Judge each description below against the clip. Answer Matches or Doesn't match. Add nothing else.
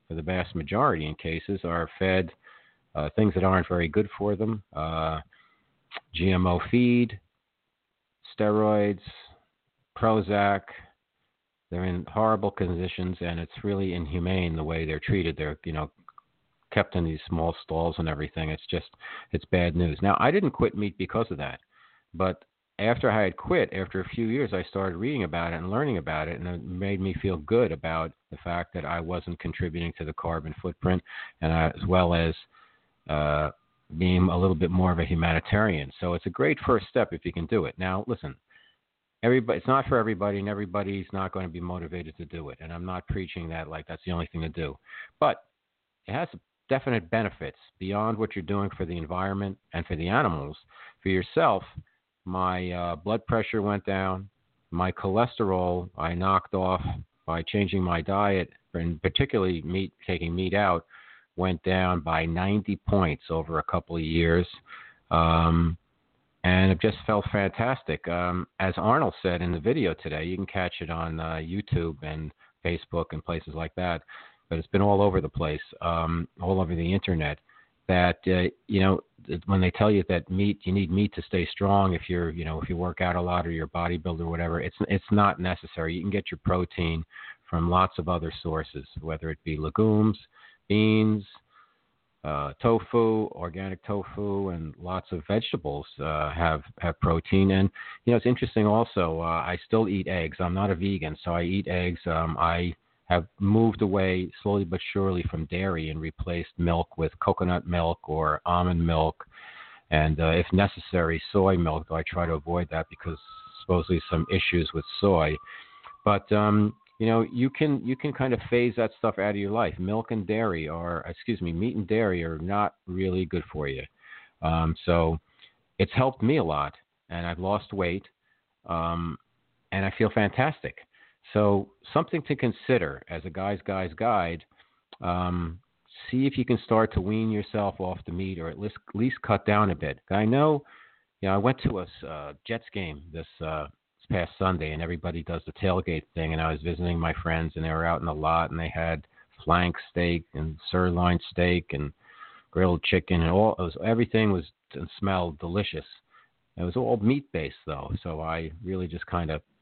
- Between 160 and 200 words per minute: Matches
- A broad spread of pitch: Doesn't match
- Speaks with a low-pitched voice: Matches